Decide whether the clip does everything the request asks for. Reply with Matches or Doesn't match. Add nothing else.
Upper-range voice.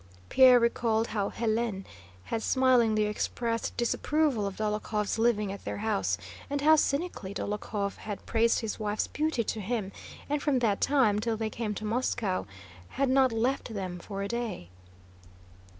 Matches